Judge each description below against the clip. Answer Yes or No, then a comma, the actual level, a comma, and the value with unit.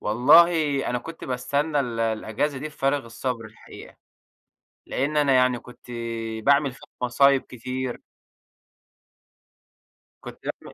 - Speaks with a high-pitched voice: No, low, 130 Hz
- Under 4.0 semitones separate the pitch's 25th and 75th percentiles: Yes, average, 2.7 semitones